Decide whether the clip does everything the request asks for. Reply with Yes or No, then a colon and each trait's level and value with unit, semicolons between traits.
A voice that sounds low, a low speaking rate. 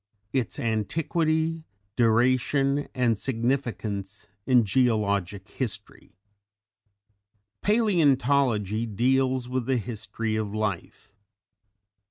Yes: low, 120 Hz; slow, 75 wpm